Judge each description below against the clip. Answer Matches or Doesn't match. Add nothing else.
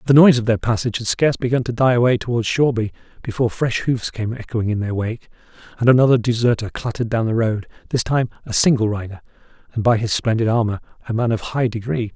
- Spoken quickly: Matches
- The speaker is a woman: Doesn't match